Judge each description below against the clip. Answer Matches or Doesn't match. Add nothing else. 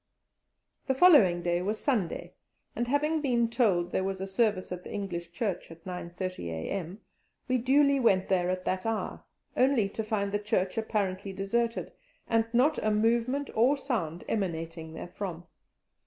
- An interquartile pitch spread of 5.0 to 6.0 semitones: Doesn't match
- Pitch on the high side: Matches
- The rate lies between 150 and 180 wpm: Matches